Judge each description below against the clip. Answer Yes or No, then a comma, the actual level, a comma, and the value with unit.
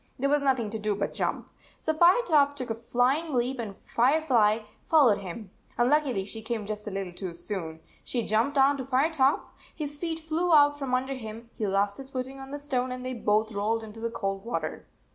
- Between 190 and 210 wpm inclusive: Yes, fast, 205 wpm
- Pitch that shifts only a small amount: No, average, 4.8 semitones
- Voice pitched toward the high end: Yes, very high, 250 Hz